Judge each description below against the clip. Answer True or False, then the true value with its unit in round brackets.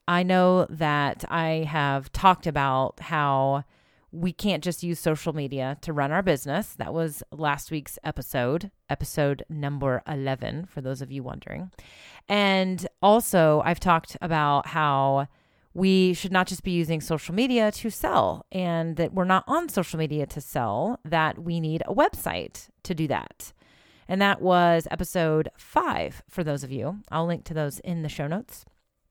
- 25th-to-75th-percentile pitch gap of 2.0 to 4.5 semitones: True (4.0 semitones)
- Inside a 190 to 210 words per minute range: False (165 wpm)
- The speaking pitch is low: False (165 Hz)